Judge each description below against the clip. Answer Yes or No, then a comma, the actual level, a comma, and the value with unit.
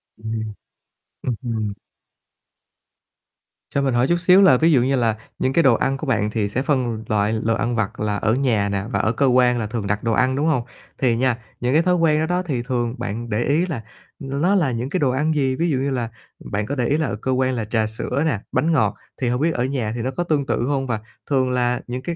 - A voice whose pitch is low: Yes, low, 125 Hz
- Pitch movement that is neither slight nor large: Yes, average, 3.7 semitones